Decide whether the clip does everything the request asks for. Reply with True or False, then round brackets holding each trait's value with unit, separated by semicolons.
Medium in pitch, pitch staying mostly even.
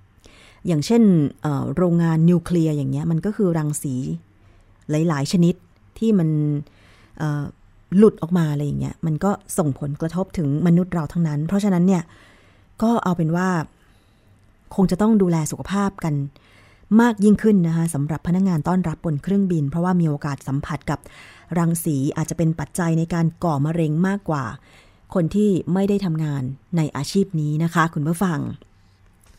False (160 Hz; 4.2 semitones)